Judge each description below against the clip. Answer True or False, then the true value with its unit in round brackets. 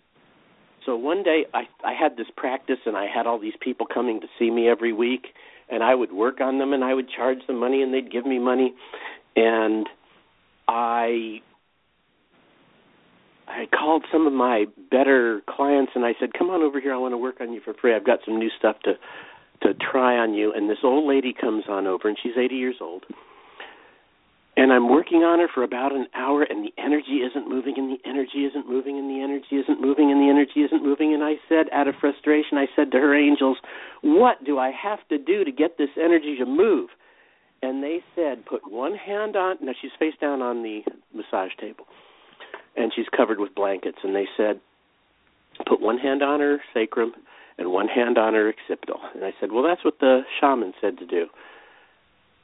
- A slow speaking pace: False (205 wpm)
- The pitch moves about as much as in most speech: True (3.8 semitones)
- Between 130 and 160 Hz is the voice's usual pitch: True (135 Hz)